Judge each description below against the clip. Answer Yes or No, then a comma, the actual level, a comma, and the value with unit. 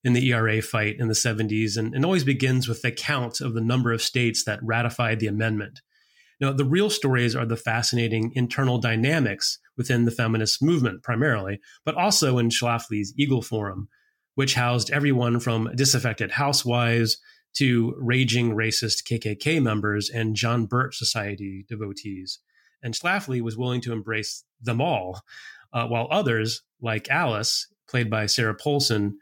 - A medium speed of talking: Yes, average, 155 wpm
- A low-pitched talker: Yes, low, 120 Hz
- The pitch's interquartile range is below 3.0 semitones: Yes, narrow, 2.6 semitones